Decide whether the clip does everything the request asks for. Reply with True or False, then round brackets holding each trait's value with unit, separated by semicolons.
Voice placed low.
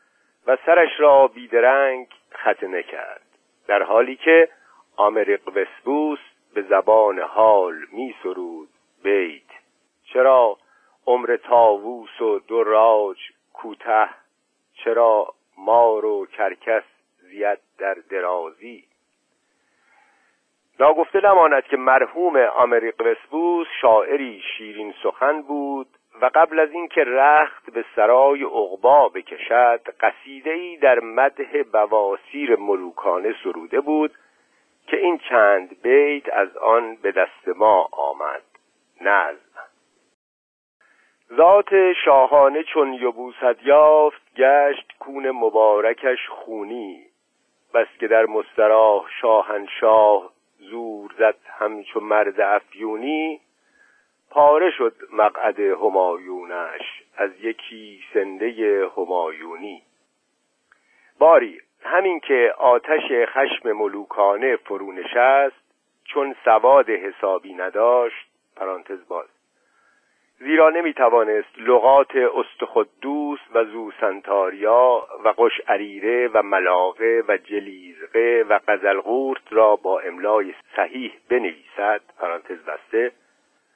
False (145 Hz)